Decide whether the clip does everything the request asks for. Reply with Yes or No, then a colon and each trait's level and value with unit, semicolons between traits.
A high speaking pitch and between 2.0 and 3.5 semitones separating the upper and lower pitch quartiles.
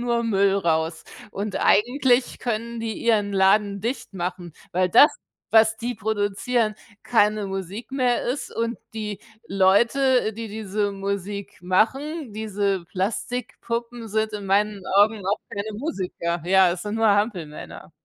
Yes: high, 210 Hz; average, 3.0 semitones